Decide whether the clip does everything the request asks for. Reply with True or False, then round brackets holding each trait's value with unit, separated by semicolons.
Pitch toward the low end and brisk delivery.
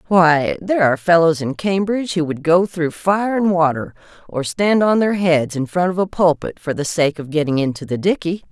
False (170 Hz; 220 wpm)